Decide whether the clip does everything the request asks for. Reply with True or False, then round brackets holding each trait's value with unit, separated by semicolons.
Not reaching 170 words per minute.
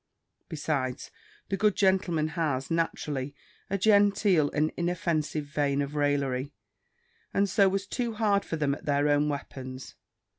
True (140 wpm)